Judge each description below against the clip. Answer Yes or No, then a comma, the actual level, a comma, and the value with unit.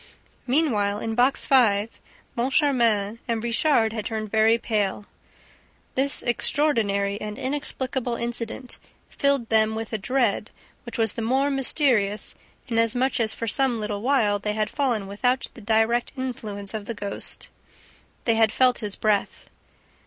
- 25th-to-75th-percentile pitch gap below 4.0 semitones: Yes, average, 3.2 semitones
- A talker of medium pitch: No, high, 230 Hz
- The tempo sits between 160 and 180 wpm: No, average, 140 wpm